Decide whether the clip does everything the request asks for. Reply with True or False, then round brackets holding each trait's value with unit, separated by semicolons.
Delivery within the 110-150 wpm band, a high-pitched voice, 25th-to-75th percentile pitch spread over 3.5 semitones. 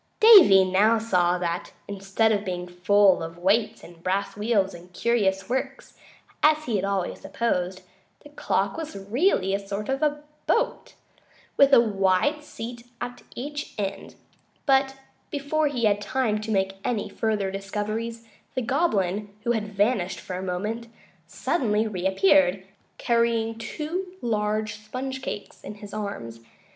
True (145 wpm; 210 Hz; 3.9 semitones)